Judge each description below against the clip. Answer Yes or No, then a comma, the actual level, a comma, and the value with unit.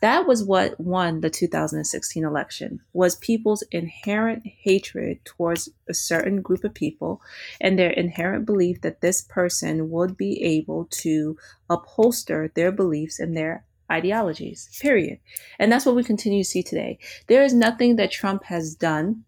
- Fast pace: No, average, 155 wpm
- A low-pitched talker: No, medium, 180 Hz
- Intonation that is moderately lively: Yes, average, 4.5 semitones